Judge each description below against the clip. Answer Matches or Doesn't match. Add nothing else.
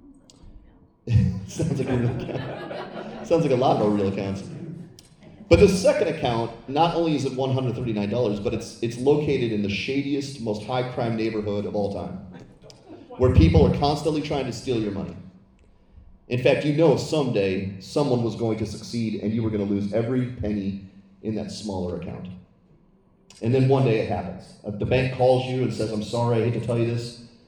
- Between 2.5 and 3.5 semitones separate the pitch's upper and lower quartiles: Doesn't match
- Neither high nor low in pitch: Doesn't match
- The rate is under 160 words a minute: Doesn't match